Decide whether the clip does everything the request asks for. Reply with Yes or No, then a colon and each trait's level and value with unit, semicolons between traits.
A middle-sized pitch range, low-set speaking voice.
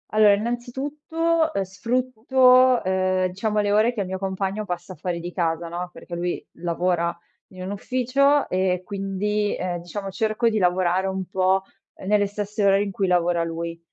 No: average, 3.2 semitones; high, 195 Hz